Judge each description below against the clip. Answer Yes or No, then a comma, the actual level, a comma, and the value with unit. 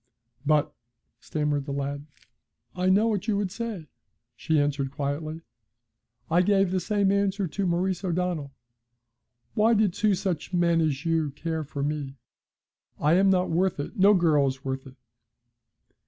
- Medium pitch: Yes, medium, 170 Hz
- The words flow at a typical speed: Yes, average, 155 wpm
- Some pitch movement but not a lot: Yes, average, 4.7 semitones